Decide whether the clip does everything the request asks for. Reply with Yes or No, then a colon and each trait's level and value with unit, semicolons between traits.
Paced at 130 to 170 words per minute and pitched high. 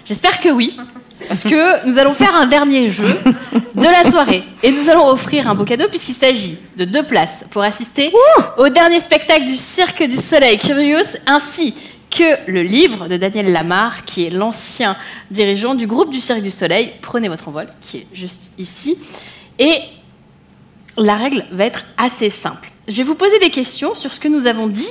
No: average, 190 wpm; very high, 250 Hz